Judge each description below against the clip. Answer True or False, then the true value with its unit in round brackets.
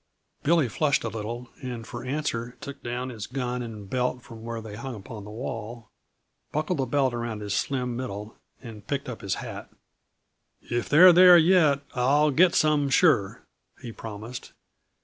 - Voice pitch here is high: False (125 Hz)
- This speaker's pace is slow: False (170 wpm)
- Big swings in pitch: False (3.9 semitones)